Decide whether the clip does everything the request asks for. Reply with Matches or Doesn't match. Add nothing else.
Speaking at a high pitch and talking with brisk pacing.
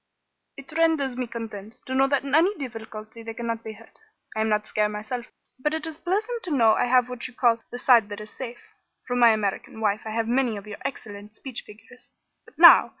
Matches